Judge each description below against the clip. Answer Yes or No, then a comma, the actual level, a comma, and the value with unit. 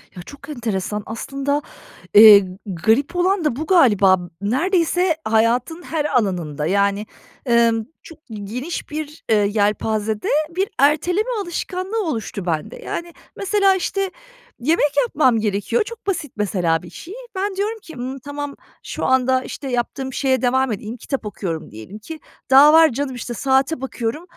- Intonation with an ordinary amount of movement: No, wide, 7.2 semitones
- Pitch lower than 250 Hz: No, very high, 260 Hz